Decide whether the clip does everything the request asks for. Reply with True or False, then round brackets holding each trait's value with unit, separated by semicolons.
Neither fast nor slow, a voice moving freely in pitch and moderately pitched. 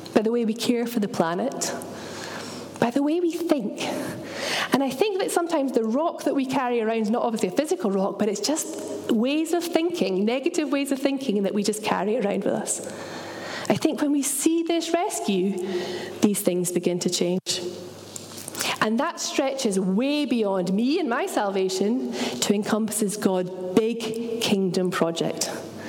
False (170 wpm; 6.6 semitones; 235 Hz)